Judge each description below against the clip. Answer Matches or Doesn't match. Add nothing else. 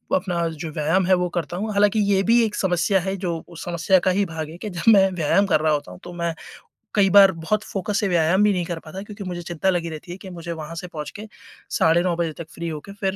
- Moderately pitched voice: Matches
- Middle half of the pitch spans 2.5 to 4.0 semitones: Matches